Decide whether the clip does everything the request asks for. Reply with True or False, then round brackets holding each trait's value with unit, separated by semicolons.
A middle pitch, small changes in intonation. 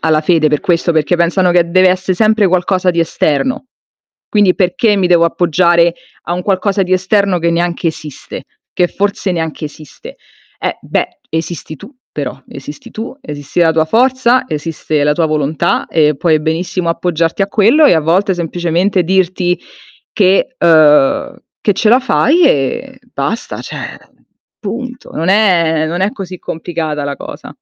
False (175 Hz; 3.6 semitones)